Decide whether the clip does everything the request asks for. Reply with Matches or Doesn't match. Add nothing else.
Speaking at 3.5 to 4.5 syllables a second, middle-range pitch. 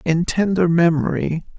Matches